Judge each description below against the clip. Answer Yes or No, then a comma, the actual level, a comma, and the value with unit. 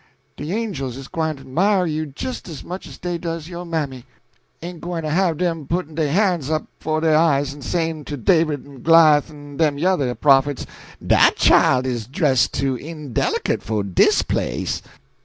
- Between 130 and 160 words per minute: No, average, 180 wpm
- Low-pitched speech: No, medium, 155 Hz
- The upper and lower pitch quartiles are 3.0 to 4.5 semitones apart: Yes, average, 3.5 semitones